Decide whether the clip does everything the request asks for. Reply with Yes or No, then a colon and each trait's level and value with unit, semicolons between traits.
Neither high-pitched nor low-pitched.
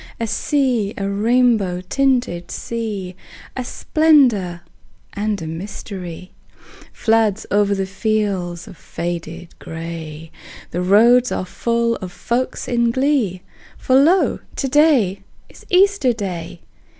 No: high, 210 Hz